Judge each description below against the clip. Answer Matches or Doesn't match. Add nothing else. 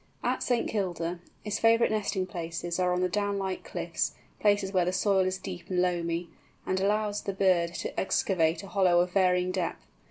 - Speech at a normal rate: Matches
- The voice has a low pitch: Doesn't match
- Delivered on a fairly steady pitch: Matches